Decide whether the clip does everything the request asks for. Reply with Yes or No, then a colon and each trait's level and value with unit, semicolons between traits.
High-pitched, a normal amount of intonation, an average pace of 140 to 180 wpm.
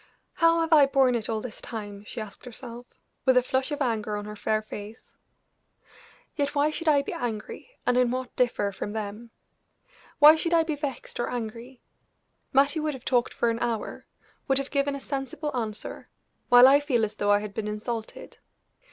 No: high, 245 Hz; average, 4.4 semitones; average, 195 wpm